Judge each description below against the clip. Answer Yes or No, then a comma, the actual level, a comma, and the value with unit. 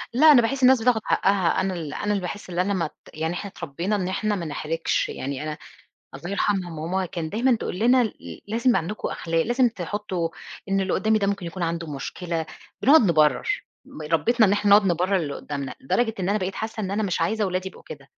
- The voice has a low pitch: No, high, 190 Hz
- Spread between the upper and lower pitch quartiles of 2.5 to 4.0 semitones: No, average, 4.4 semitones